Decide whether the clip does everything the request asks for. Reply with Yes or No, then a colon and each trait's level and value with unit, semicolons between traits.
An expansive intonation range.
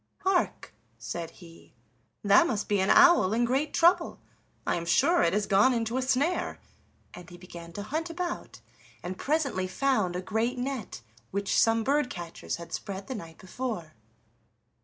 Yes: wide, 6.7 semitones